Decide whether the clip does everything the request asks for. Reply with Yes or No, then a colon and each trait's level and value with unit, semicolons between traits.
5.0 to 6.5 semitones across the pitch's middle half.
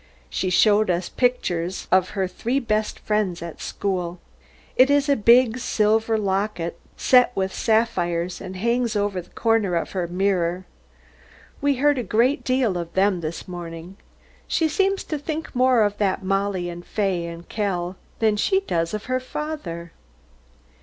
Yes: wide, 5.5 semitones